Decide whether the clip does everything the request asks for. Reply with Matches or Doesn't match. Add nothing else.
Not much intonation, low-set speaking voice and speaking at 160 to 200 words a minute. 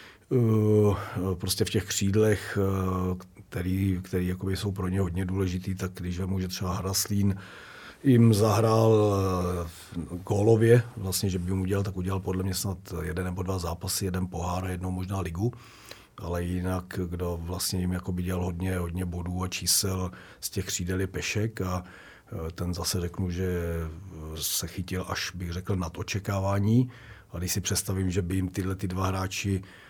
Matches